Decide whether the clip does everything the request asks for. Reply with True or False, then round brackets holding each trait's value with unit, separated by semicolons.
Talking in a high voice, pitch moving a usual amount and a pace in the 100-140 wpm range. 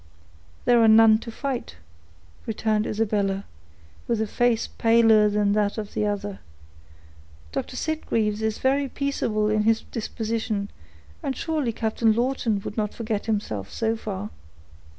False (220 Hz; 1.7 semitones; 135 wpm)